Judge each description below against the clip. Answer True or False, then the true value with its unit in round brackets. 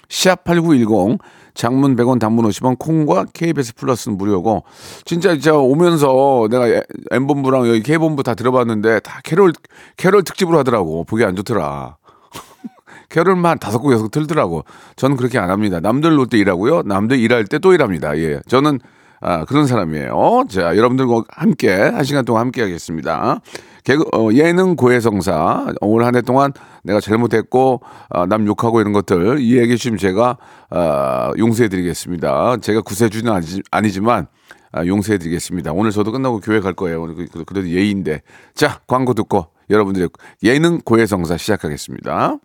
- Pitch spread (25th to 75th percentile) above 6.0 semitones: False (5.2 semitones)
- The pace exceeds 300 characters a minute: True (350 characters per minute)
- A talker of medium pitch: False (115 Hz)